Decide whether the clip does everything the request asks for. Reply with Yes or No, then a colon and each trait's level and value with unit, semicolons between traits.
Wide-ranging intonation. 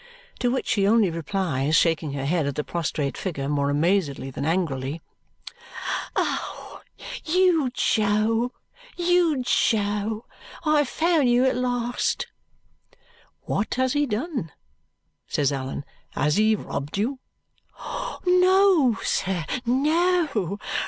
Yes: wide, 8.9 semitones